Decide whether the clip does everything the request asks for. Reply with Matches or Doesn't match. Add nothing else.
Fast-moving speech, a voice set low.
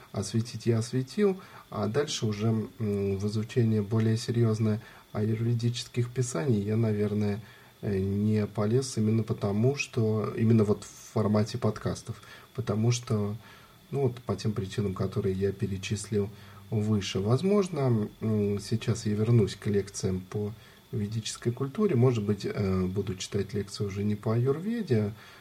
Doesn't match